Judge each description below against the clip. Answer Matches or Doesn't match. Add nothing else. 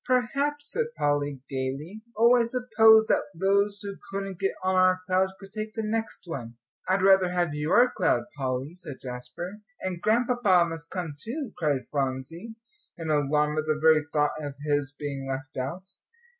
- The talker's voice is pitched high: Doesn't match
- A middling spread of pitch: Doesn't match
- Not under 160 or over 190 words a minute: Matches